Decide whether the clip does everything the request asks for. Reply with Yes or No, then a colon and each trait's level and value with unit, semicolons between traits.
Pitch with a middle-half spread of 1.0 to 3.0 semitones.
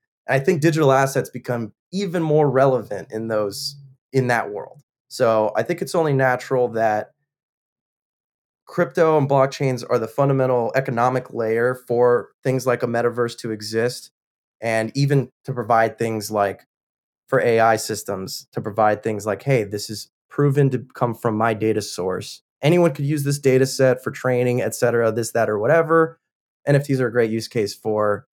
No: average, 3.7 semitones